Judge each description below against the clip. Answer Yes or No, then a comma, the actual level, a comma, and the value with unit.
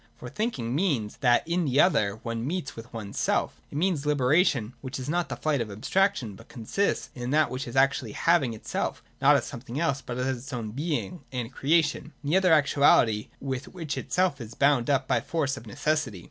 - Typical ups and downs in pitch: Yes, average, 4.6 semitones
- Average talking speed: No, fast, 220 wpm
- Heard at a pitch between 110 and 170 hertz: Yes, low, 135 Hz